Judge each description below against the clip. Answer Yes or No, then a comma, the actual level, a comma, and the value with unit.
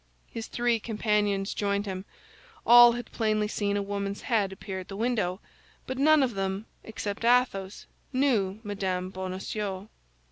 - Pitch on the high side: Yes, high, 205 Hz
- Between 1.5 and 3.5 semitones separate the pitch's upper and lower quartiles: Yes, average, 3.1 semitones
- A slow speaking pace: No, average, 145 wpm